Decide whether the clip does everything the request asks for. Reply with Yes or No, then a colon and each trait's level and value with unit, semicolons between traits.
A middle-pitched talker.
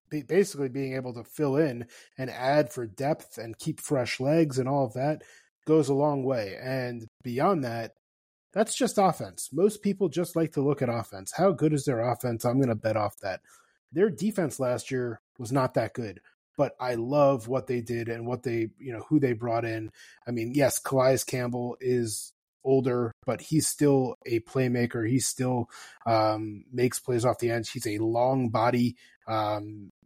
No: low, 125 Hz